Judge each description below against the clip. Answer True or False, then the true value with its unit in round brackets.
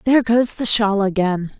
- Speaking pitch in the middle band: False (215 Hz)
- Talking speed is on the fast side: False (190 wpm)